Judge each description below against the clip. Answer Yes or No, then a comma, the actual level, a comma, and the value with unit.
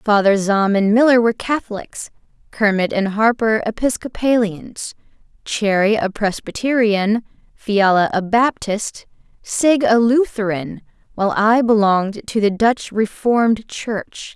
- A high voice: Yes, high, 215 Hz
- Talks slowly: Yes, slow, 115 wpm